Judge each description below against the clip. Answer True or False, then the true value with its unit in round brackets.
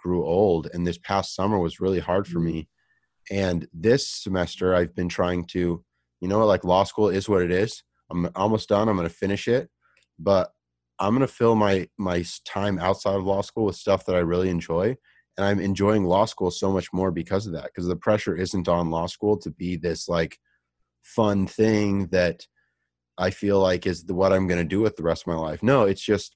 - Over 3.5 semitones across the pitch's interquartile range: False (2.6 semitones)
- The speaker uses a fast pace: True (220 wpm)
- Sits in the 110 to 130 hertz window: False (95 Hz)